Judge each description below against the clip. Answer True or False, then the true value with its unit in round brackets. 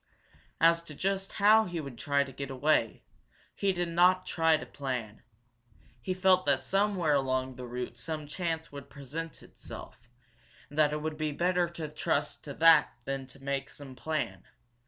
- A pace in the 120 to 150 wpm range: False (175 wpm)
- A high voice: False (150 Hz)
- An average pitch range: True (4.0 semitones)